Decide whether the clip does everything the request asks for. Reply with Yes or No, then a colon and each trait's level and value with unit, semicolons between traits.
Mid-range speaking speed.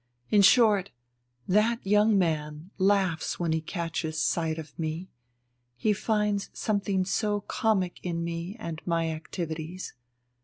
No: slow, 125 wpm